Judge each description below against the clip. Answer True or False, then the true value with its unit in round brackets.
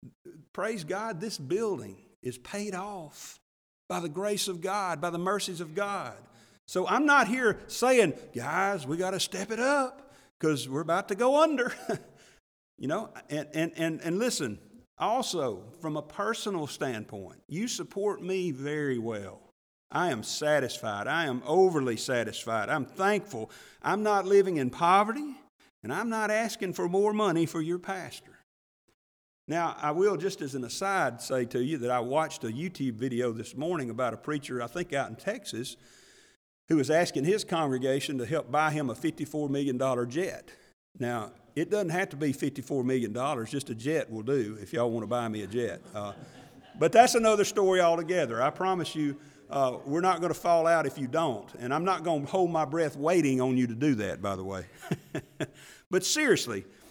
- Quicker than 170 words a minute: True (185 wpm)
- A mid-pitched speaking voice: True (160 Hz)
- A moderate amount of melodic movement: False (7.0 semitones)